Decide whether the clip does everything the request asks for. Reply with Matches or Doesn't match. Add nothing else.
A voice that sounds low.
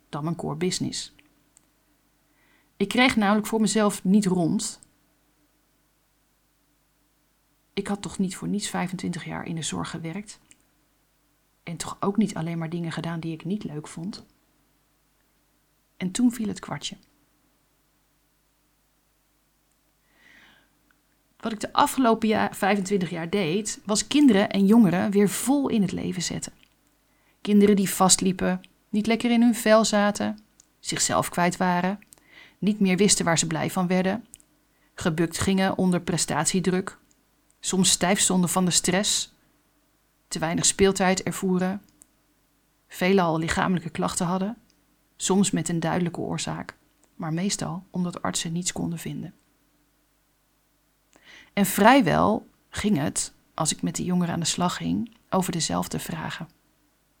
Doesn't match